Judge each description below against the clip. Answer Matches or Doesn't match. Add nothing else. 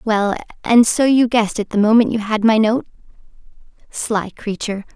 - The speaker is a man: Doesn't match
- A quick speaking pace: Doesn't match